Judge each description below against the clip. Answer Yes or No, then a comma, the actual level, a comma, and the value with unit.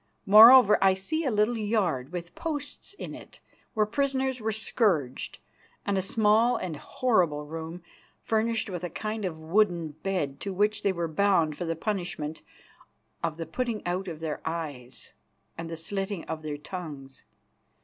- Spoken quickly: No, average, 160 wpm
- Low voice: No, medium, 185 Hz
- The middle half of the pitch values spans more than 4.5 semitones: Yes, average, 5.0 semitones